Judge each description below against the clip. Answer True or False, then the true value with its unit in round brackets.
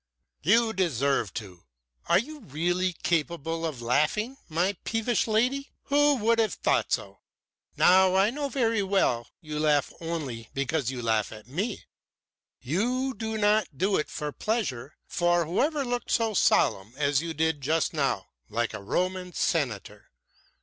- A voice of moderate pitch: True (175 Hz)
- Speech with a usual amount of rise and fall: False (7.6 semitones)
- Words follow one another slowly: False (155 wpm)